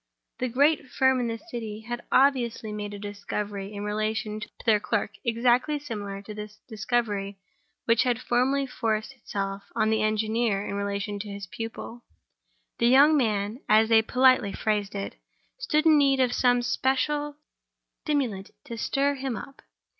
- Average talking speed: Yes, average, 160 wpm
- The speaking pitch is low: No, high, 225 Hz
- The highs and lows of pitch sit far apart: No, average, 3.8 semitones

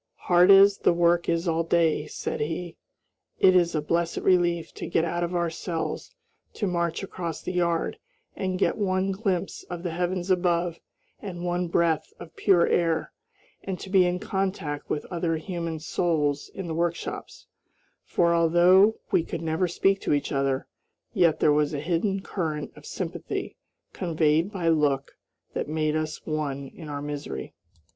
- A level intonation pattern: Yes, narrow, 2.2 semitones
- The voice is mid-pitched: Yes, medium, 170 Hz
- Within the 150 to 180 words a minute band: Yes, average, 165 wpm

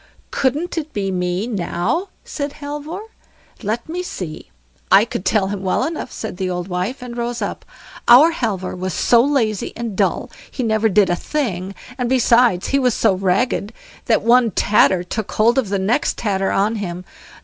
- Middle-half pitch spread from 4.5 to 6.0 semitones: Yes, average, 4.9 semitones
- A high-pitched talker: Yes, high, 220 Hz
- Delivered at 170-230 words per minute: Yes, average, 180 wpm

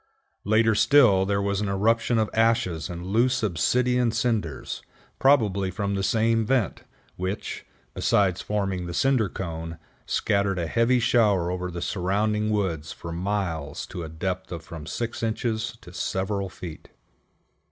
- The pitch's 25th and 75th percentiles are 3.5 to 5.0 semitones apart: Yes, average, 3.9 semitones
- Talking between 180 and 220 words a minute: No, average, 145 wpm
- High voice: No, low, 100 Hz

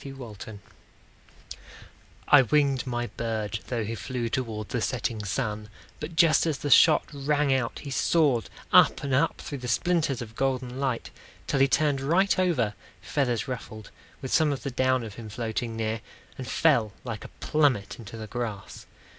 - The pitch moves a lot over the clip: No, average, 3.9 semitones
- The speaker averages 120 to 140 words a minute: No, average, 170 wpm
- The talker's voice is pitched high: No, low, 125 Hz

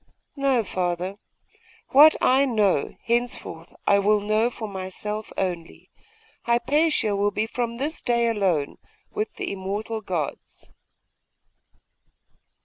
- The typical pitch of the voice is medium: No, high, 215 Hz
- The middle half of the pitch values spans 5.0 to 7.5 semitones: No, average, 3.7 semitones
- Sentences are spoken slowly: Yes, slow, 110 wpm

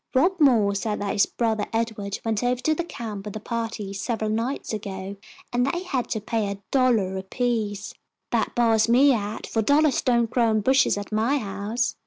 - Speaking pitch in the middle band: No, high, 225 Hz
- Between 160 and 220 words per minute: Yes, average, 195 wpm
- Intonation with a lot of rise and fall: No, average, 3.2 semitones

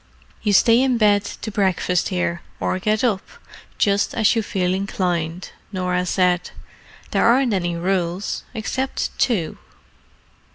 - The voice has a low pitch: No, high, 195 Hz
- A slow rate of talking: Yes, slow, 130 wpm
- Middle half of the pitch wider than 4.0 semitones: No, average, 3.2 semitones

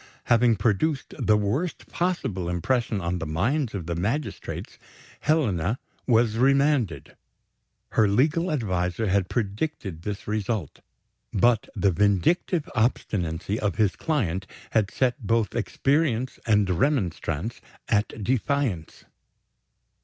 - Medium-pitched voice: No, low, 110 Hz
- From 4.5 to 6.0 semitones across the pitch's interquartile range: Yes, wide, 5.6 semitones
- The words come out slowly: Yes, slow, 110 wpm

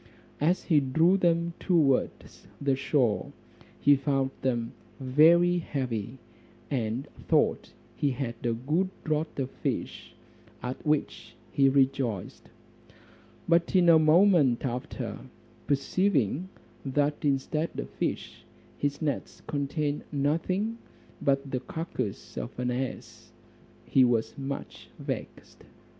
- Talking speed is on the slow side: Yes, slow, 115 wpm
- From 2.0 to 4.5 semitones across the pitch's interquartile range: Yes, average, 3.7 semitones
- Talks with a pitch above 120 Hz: Yes, medium, 140 Hz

